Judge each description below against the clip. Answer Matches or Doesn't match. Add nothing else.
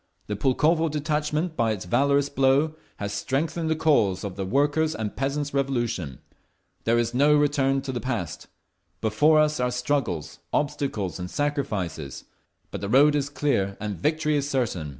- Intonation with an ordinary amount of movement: Doesn't match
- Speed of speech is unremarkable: Matches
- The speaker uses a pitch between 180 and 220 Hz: Doesn't match